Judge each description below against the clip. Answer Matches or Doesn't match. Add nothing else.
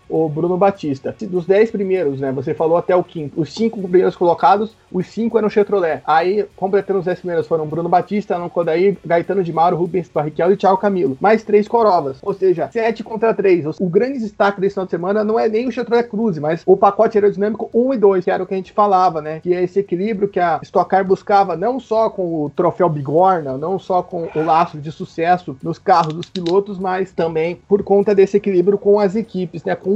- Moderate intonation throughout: Matches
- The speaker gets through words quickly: Matches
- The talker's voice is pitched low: Doesn't match